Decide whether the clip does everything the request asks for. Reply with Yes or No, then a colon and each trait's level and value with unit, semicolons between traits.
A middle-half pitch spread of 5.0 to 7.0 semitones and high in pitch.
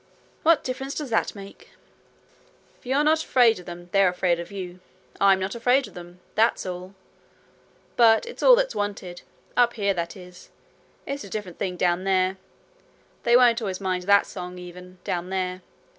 No: average, 4.6 semitones; high, 195 Hz